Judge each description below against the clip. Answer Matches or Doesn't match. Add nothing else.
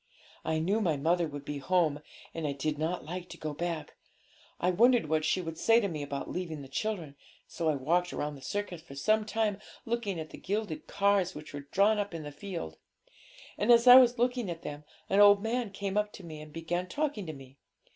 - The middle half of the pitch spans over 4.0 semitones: Matches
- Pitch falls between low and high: Matches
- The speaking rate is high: Matches